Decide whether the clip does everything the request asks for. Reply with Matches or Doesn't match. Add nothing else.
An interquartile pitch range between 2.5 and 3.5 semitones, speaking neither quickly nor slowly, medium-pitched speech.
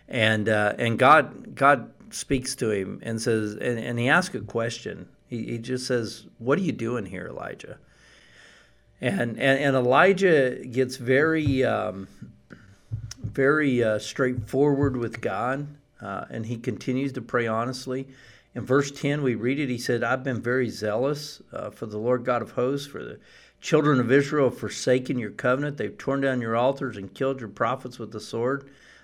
Doesn't match